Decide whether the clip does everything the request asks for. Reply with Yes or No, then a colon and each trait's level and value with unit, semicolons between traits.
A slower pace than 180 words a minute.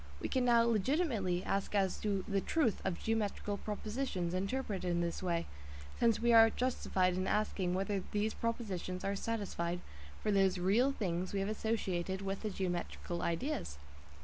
Yes: average, 160 wpm